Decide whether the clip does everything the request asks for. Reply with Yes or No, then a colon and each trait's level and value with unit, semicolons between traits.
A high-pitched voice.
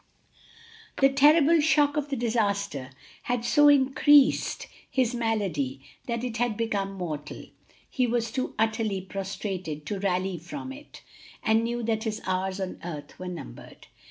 Yes: high, 220 Hz